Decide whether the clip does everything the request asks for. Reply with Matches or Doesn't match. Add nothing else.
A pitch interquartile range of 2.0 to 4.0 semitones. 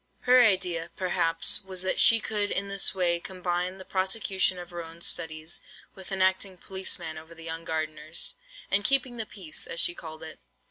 Matches